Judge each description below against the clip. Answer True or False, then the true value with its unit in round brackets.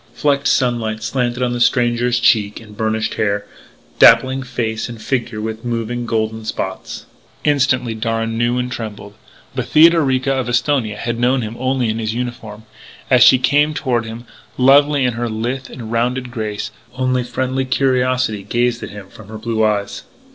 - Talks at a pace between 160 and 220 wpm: True (165 wpm)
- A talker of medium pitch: False (120 Hz)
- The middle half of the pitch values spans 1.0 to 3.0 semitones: True (2.6 semitones)